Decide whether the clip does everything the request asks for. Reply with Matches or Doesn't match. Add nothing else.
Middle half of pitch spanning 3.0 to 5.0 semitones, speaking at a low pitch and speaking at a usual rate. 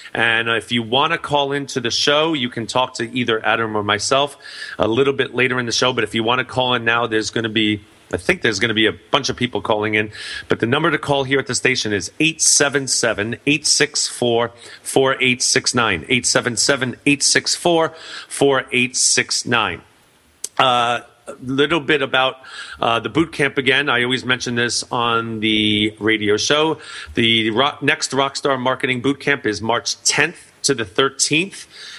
Matches